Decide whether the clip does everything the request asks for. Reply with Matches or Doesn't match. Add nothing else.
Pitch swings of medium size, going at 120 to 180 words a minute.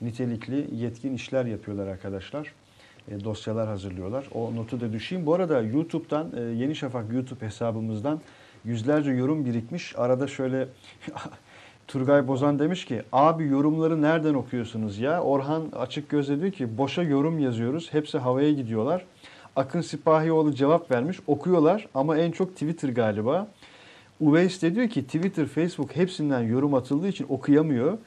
Matches